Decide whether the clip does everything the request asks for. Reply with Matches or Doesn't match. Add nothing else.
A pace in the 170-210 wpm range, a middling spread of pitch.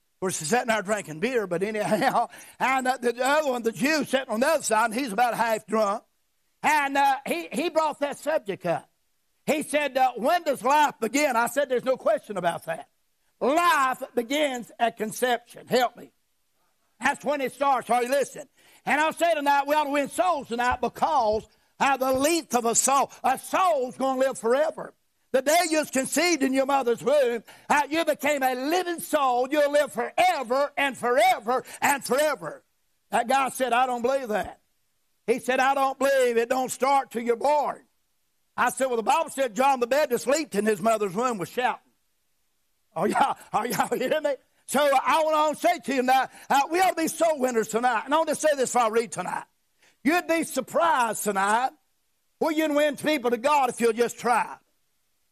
Matches